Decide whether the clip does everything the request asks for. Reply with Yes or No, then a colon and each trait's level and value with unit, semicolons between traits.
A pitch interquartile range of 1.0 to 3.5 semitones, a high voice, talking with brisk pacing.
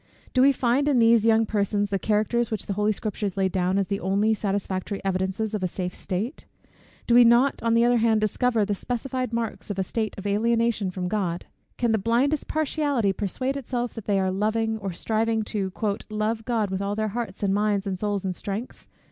Yes: average, 2.9 semitones; high, 215 Hz; fast, 210 wpm